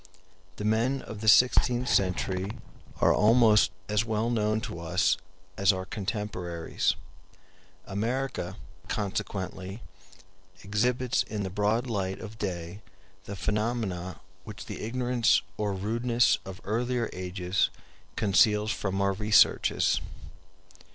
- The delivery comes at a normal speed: No, slow, 110 wpm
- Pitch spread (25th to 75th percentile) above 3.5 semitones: No, average, 3.1 semitones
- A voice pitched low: Yes, low, 105 Hz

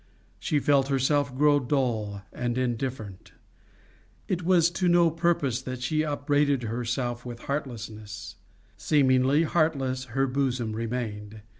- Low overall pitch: Yes, low, 130 Hz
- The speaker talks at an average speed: No, slow, 120 wpm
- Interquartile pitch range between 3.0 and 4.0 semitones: Yes, average, 3.6 semitones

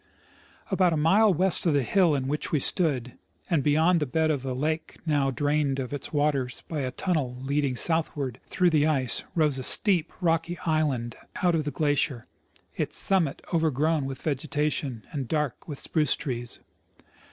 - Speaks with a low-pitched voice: No, medium, 150 Hz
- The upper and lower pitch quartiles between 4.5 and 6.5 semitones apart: No, average, 3.2 semitones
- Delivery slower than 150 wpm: No, average, 175 wpm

